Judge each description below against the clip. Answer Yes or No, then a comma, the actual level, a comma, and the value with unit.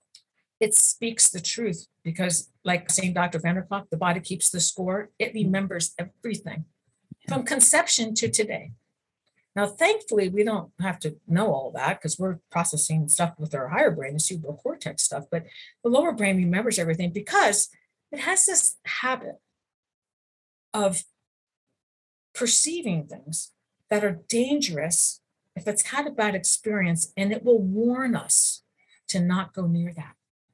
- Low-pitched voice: No, high, 190 Hz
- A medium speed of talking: Yes, average, 145 wpm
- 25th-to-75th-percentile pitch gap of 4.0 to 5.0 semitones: Yes, average, 4.4 semitones